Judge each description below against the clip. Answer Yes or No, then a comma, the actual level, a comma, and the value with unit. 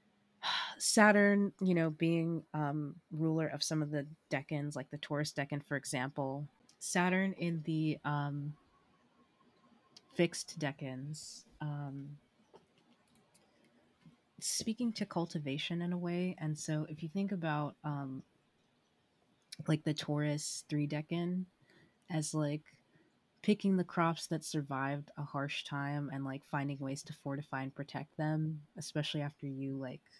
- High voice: No, medium, 150 Hz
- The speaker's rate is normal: No, slow, 130 wpm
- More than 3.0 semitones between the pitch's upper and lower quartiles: No, average, 2.7 semitones